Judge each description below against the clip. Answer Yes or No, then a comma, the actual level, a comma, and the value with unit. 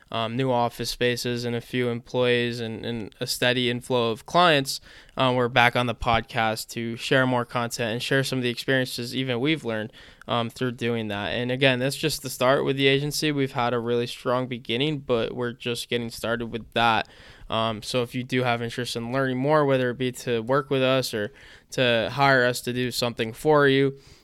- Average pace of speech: No, fast, 215 wpm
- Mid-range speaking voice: No, low, 125 Hz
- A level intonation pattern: Yes, narrow, 2.0 semitones